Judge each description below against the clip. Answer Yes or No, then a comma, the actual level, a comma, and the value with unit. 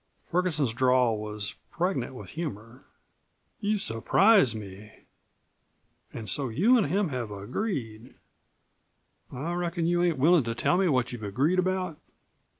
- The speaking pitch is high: No, medium, 140 Hz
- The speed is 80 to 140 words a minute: Yes, slow, 135 wpm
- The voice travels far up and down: Yes, wide, 7.6 semitones